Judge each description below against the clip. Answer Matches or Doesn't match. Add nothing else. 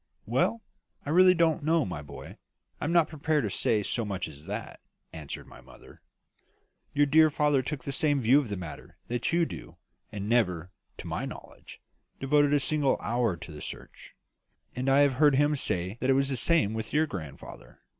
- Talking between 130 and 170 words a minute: Doesn't match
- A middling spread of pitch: Doesn't match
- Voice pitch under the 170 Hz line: Matches